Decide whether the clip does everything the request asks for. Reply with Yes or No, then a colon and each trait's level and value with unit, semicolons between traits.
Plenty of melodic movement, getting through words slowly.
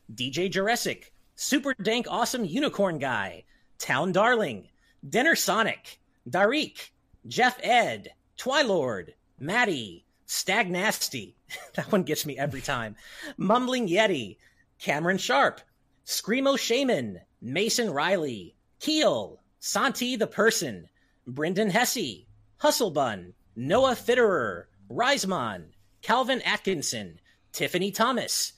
Yes: wide, 8.2 semitones; slow, 95 wpm